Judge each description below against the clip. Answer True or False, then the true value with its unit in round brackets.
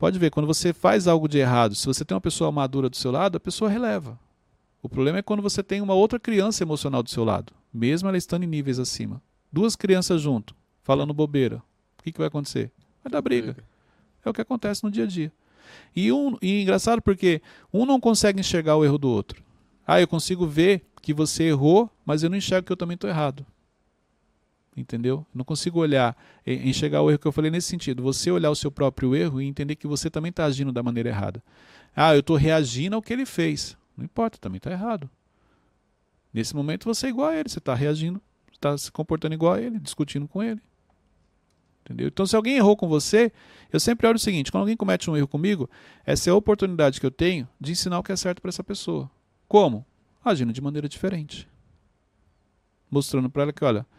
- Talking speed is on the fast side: True (215 wpm)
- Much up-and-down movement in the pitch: True (6.3 semitones)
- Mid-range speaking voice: True (155 Hz)